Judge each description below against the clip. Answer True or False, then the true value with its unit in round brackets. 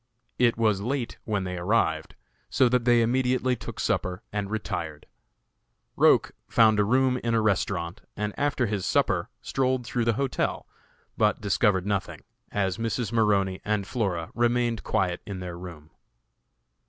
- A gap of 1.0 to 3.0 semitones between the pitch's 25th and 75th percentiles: False (4.0 semitones)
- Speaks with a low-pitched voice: True (105 Hz)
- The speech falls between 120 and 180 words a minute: True (150 wpm)